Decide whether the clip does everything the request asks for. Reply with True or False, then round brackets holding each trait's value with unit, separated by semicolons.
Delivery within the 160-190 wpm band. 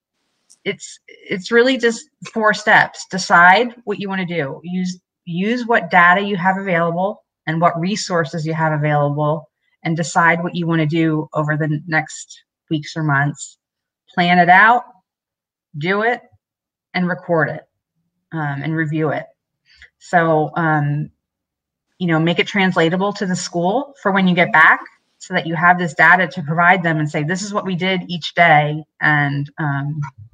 True (170 wpm)